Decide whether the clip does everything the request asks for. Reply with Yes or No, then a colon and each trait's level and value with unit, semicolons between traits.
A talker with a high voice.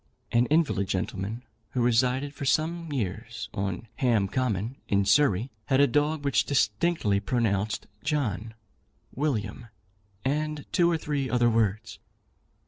No: low, 125 Hz